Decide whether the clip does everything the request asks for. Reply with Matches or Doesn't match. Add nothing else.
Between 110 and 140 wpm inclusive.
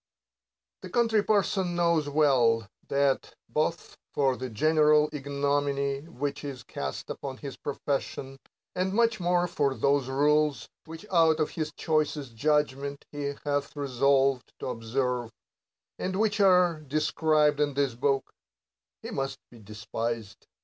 Matches